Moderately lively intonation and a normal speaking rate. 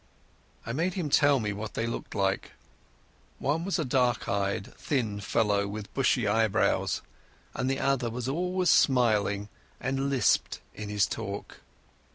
Yes: average, 4.9 semitones; average, 145 wpm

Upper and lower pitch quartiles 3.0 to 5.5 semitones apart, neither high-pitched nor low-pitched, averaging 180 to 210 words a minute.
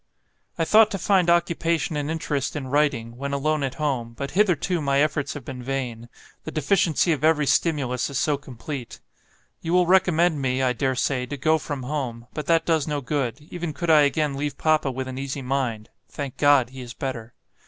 Yes: average, 3.3 semitones; medium, 145 Hz; average, 200 wpm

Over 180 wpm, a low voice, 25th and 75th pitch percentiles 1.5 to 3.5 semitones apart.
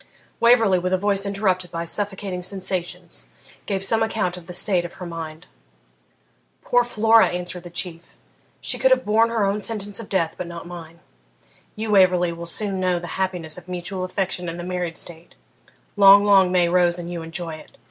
No: average, 190 wpm; medium, 185 Hz; average, 2.7 semitones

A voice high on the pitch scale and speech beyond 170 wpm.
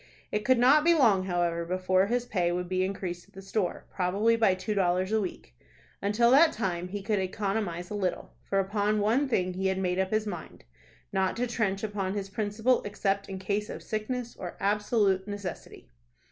Yes: high, 200 Hz; average, 195 wpm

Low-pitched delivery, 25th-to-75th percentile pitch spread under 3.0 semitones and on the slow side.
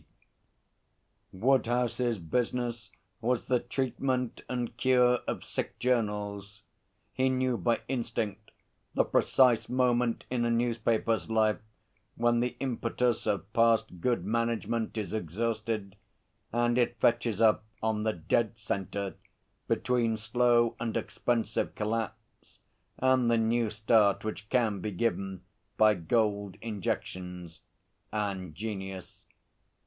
Yes: low, 115 Hz; narrow, 2.4 semitones; slow, 115 wpm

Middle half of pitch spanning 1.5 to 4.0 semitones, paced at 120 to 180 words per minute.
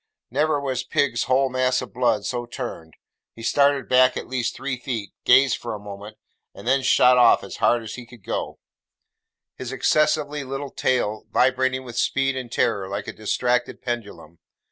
Yes: narrow, 2.5 semitones; average, 175 wpm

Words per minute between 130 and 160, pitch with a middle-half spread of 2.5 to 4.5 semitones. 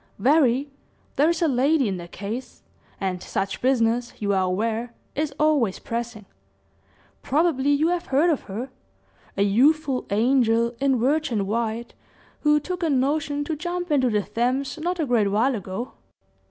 No: average, 155 wpm; average, 5.0 semitones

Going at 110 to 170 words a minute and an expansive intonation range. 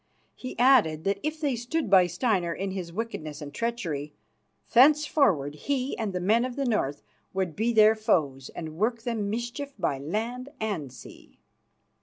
Yes: average, 165 wpm; wide, 6.4 semitones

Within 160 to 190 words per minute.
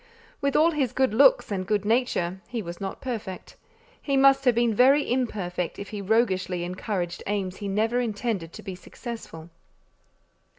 Yes: average, 165 wpm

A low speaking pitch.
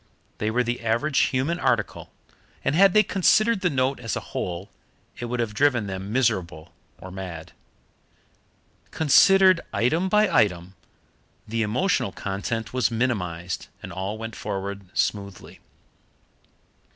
Yes: low, 115 Hz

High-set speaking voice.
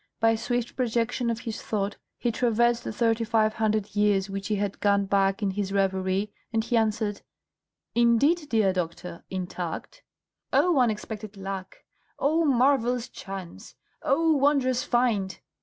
Yes: high, 220 Hz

